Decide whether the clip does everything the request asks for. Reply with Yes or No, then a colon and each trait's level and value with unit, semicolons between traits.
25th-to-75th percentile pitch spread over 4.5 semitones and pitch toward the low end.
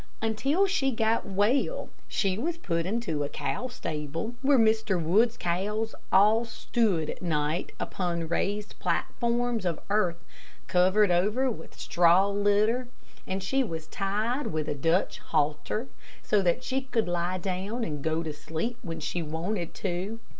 No: average, 5.1 semitones; high, 200 Hz